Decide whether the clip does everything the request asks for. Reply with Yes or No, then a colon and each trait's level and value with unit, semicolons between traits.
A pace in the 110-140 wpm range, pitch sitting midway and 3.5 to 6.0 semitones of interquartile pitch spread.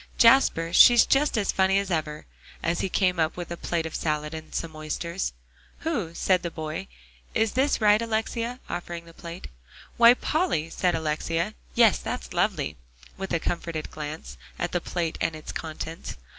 No: average, 170 wpm; medium, 170 Hz; average, 4.1 semitones